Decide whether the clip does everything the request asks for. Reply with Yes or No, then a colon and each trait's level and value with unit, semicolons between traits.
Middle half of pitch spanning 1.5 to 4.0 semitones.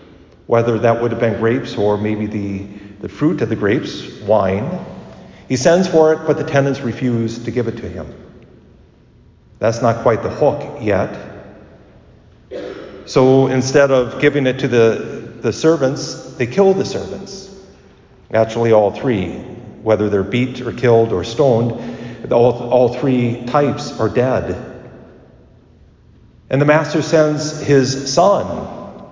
No: average, 4.5 semitones